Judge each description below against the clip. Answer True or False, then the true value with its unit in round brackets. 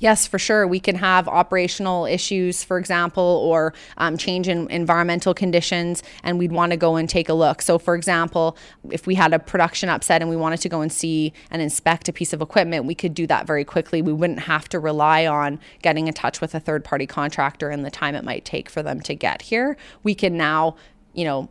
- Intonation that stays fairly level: True (2.2 semitones)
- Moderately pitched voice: True (170 Hz)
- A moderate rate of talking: False (230 wpm)